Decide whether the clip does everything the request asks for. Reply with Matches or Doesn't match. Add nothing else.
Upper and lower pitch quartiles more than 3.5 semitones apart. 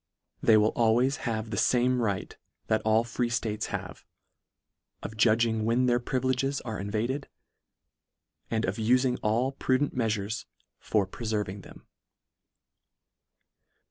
Doesn't match